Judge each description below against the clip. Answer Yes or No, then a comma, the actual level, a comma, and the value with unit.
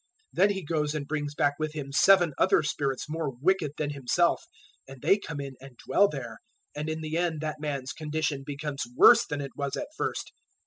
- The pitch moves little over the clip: Yes, narrow, 2.2 semitones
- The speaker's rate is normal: No, fast, 210 wpm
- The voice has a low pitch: No, medium, 150 Hz